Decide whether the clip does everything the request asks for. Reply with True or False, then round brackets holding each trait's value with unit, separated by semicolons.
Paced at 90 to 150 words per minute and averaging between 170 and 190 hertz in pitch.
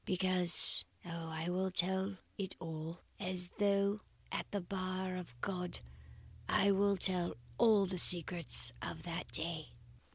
True (135 wpm; 185 Hz)